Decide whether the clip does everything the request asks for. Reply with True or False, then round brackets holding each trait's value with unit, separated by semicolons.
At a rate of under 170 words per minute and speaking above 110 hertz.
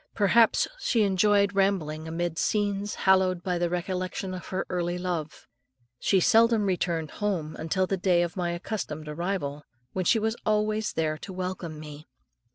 True (160 wpm; 185 Hz)